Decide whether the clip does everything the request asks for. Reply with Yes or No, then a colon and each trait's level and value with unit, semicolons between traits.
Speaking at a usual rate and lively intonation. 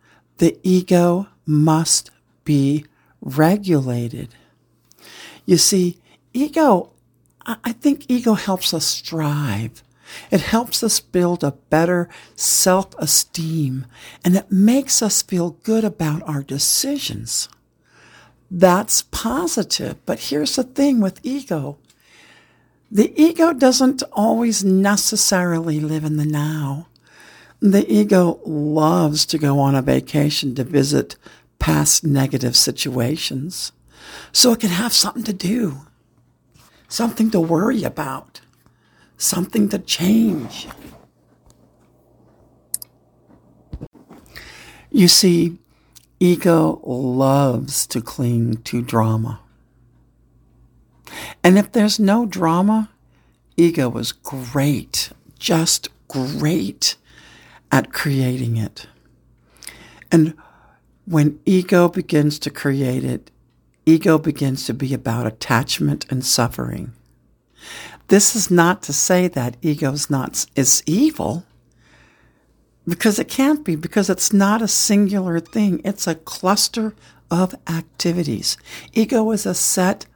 No: slow, 105 wpm; wide, 6.6 semitones